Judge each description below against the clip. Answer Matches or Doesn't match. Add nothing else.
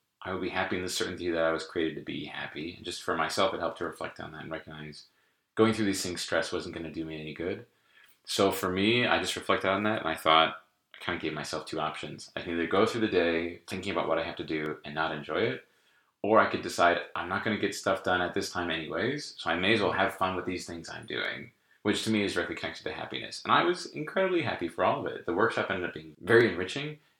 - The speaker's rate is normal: Doesn't match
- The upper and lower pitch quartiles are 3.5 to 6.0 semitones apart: Matches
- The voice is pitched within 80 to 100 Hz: Matches